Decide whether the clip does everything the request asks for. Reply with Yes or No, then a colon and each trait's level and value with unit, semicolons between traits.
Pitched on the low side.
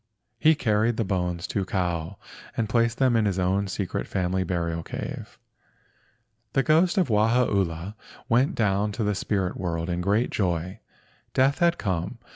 Yes: low, 100 Hz